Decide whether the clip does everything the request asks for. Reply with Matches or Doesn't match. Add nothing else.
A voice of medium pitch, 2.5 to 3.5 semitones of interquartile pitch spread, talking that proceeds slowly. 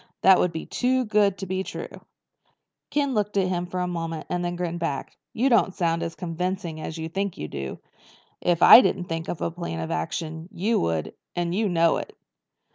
Doesn't match